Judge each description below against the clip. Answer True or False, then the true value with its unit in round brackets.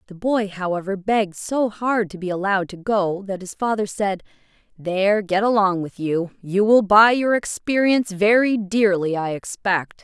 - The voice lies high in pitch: True (200 Hz)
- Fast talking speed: False (175 wpm)